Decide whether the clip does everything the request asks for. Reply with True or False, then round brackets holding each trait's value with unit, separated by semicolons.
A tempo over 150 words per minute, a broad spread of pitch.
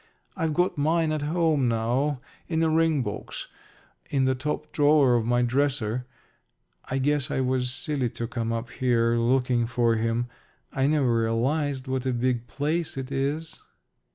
False (160 wpm; 3.7 semitones)